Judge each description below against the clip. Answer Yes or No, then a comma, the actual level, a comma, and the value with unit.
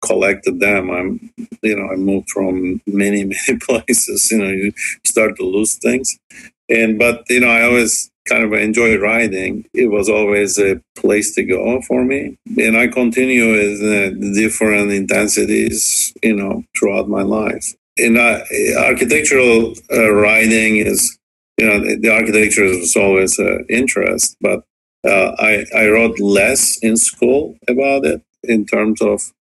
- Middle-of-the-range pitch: No, low, 110 Hz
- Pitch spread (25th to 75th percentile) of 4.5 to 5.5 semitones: No, narrow, 2.6 semitones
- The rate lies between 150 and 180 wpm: Yes, average, 160 wpm